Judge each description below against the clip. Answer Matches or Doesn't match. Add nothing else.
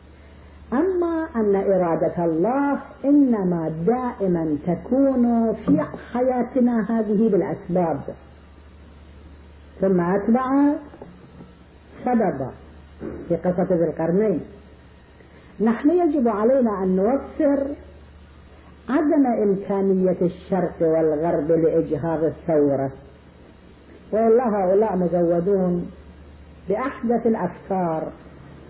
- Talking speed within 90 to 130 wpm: Doesn't match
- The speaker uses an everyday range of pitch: Doesn't match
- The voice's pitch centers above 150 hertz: Matches